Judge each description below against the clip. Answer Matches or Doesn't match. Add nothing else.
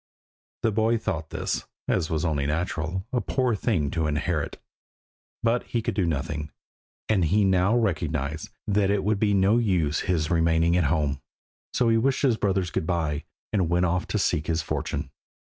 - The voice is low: Matches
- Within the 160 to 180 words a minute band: Matches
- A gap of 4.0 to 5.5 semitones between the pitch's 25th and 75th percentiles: Matches